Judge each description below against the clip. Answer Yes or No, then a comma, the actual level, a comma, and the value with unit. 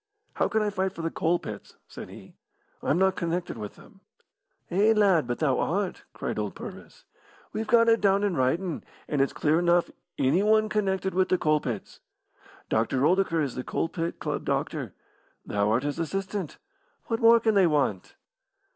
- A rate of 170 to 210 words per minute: Yes, average, 180 wpm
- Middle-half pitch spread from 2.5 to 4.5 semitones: No, wide, 5.4 semitones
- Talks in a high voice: No, medium, 175 Hz